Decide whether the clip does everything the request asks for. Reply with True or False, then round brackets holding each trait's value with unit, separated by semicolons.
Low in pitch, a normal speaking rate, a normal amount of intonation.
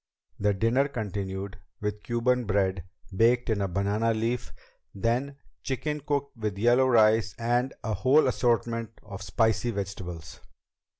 False (115 Hz; 130 wpm; 3.5 semitones)